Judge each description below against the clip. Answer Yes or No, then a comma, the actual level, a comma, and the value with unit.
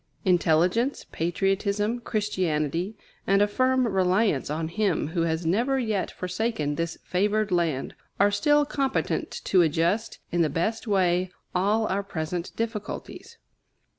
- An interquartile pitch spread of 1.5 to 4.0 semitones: No, average, 4.4 semitones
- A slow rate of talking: Yes, slow, 130 wpm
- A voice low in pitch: No, high, 190 Hz